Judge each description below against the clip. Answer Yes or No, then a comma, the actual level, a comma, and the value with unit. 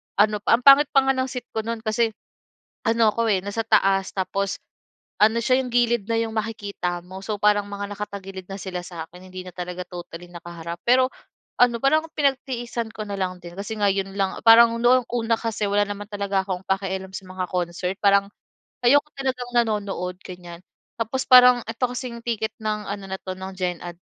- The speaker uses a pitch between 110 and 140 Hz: No, high, 205 Hz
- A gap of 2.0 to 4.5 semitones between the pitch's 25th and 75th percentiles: Yes, average, 3.8 semitones